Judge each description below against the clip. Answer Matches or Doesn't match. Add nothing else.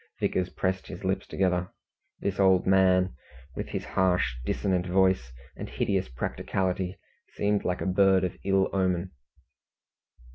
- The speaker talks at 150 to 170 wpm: Doesn't match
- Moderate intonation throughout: Doesn't match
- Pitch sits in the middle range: Doesn't match